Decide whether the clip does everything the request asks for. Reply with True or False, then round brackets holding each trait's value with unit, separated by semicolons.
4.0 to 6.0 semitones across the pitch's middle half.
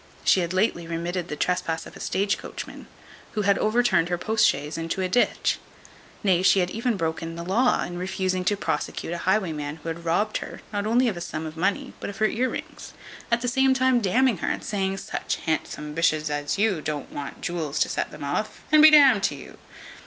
True (4.8 semitones)